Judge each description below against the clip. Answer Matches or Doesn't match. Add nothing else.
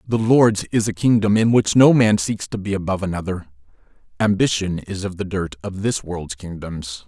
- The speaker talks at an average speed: Matches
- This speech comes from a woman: Doesn't match